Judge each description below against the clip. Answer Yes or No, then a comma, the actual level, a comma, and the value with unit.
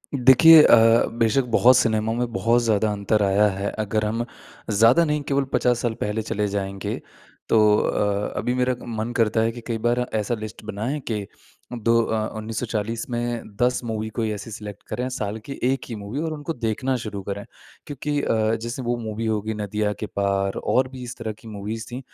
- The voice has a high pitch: No, low, 110 Hz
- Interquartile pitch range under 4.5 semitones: Yes, narrow, 2.4 semitones